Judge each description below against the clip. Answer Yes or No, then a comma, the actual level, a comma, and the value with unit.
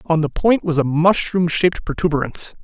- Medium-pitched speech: Yes, medium, 165 Hz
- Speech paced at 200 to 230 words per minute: No, average, 180 wpm